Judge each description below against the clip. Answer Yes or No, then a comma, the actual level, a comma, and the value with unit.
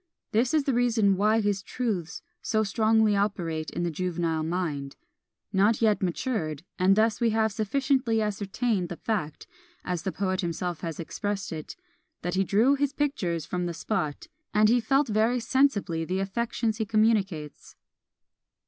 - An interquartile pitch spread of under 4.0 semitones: No, average, 4.3 semitones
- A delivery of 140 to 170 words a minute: Yes, average, 155 wpm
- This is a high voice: Yes, high, 205 Hz